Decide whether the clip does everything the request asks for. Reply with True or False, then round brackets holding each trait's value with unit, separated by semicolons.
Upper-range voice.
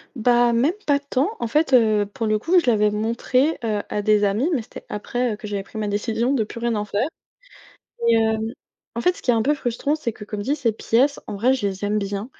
True (225 Hz)